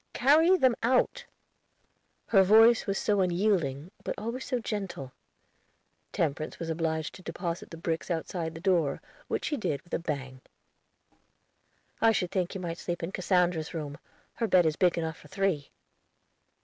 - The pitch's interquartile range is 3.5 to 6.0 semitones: Yes, average, 4.2 semitones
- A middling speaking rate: Yes, average, 160 wpm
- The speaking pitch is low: No, medium, 175 Hz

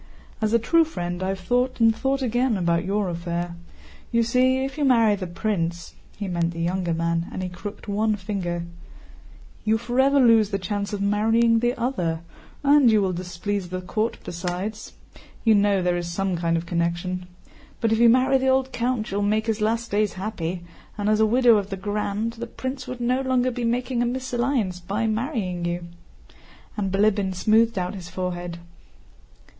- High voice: Yes, high, 210 Hz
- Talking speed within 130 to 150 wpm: No, average, 180 wpm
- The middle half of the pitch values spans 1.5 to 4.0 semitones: No, average, 4.7 semitones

